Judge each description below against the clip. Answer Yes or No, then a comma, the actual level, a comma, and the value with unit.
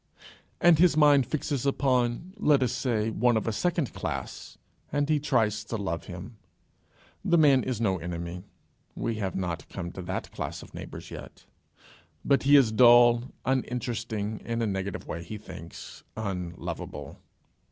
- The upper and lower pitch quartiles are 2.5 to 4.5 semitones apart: No, wide, 5.6 semitones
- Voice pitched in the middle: No, low, 115 Hz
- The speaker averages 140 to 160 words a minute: Yes, average, 155 wpm